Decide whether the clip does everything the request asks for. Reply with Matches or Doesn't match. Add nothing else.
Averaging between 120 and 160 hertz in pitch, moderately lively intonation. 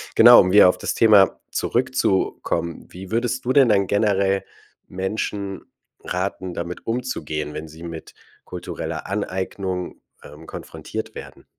Doesn't match